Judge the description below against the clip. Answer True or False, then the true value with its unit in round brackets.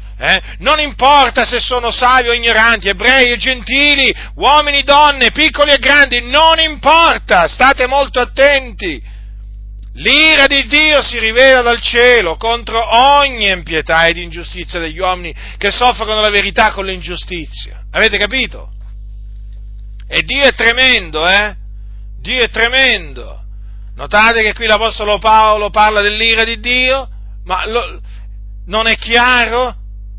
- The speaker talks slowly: False (130 wpm)